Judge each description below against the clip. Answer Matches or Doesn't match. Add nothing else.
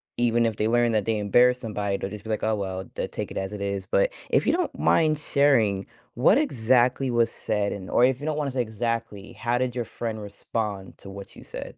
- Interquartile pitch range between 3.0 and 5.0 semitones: Matches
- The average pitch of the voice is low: Matches